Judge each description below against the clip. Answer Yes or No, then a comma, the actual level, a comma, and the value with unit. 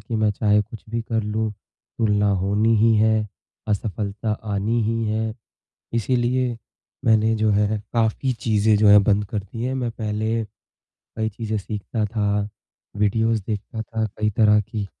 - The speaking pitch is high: No, low, 110 Hz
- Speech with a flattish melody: Yes, narrow, 1.4 semitones